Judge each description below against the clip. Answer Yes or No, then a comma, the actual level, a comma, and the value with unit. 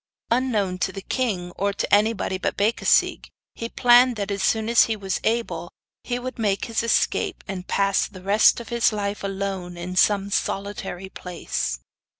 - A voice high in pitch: Yes, high, 200 Hz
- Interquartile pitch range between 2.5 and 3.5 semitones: Yes, average, 3.2 semitones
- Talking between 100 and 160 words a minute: No, average, 170 wpm